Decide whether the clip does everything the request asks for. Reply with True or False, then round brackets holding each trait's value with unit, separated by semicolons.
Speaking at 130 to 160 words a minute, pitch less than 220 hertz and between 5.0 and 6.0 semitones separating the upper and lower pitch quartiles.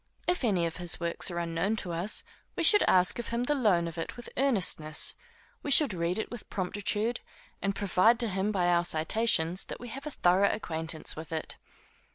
False (205 wpm; 190 Hz; 5.3 semitones)